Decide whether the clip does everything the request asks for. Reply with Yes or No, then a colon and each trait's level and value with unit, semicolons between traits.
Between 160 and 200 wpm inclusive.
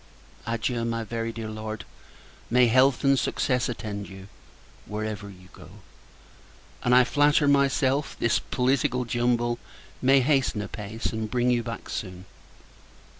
No: slow, 135 wpm